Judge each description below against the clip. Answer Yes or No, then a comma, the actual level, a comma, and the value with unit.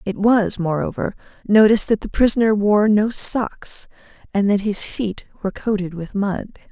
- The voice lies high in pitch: Yes, high, 205 Hz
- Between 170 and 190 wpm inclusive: No, average, 160 wpm